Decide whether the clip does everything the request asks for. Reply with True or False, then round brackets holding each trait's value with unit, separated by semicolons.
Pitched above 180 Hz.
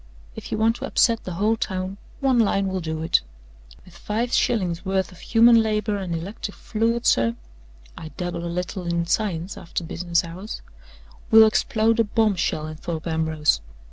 True (190 Hz)